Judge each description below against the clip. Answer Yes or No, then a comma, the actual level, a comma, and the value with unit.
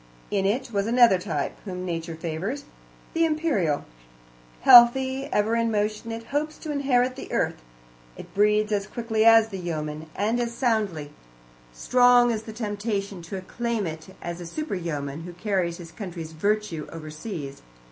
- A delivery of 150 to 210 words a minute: Yes, average, 155 wpm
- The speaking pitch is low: No, high, 205 Hz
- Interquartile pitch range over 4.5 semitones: Yes, wide, 5.6 semitones